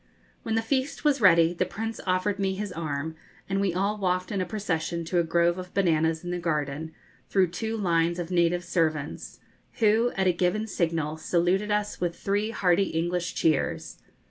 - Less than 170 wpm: No, average, 185 wpm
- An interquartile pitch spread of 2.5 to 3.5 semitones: Yes, average, 3.2 semitones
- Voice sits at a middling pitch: Yes, medium, 180 Hz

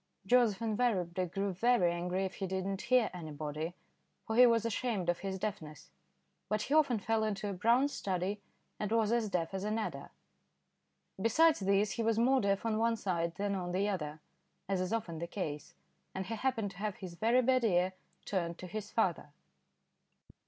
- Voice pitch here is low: No, high, 200 Hz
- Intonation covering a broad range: No, average, 4.0 semitones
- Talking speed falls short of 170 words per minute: No, average, 190 wpm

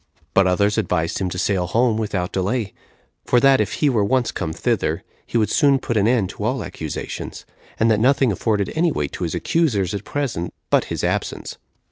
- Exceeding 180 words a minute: Yes, average, 200 wpm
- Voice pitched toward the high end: No, low, 105 Hz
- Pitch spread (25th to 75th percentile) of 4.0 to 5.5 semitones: Yes, average, 5.1 semitones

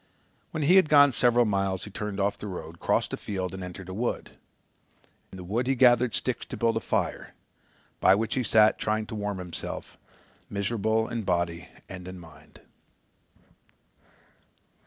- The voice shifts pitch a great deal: No, average, 4.0 semitones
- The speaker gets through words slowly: No, average, 170 wpm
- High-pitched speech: No, low, 105 Hz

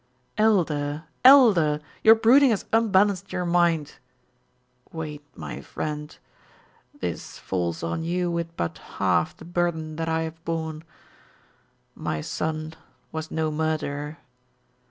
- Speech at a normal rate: No, slow, 115 wpm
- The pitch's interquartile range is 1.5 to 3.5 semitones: Yes, average, 2.7 semitones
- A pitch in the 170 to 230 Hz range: No, medium, 160 Hz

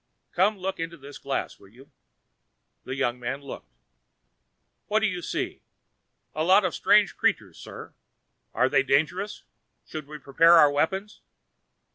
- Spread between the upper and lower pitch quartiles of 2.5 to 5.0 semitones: No, wide, 5.5 semitones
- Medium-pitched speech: Yes, medium, 155 Hz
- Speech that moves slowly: No, average, 145 wpm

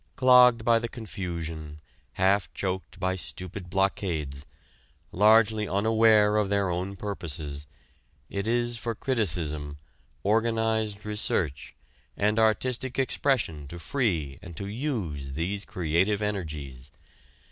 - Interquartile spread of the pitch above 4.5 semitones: Yes, average, 5.1 semitones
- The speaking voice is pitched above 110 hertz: No, low, 100 Hz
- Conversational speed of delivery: No, slow, 110 wpm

